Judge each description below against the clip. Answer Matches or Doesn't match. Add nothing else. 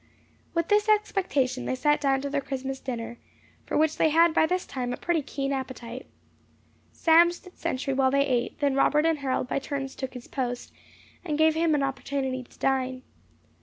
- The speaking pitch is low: Doesn't match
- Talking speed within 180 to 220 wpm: Matches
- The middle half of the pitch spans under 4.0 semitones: Matches